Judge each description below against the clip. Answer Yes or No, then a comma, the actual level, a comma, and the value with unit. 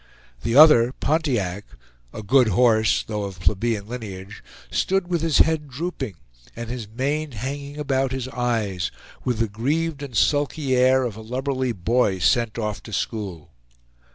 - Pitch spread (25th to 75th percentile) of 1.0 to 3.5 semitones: No, average, 4.7 semitones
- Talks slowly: No, average, 155 wpm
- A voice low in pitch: Yes, low, 125 Hz